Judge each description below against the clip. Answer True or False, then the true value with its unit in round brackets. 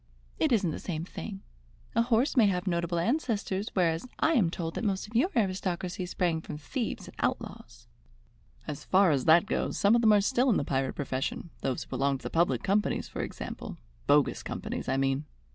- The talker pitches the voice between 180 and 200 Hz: True (185 Hz)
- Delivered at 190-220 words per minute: True (200 wpm)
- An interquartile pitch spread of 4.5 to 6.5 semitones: True (5.3 semitones)